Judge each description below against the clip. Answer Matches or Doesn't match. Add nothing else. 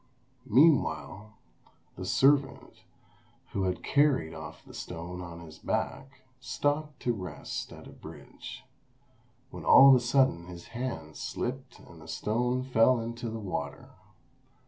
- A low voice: Matches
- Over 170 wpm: Doesn't match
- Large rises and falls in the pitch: Matches